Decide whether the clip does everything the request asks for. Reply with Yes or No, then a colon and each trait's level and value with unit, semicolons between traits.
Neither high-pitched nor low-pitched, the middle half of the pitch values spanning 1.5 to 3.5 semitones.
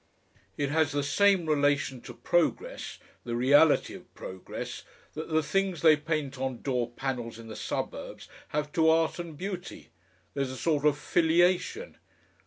No: medium, 150 Hz; average, 3.9 semitones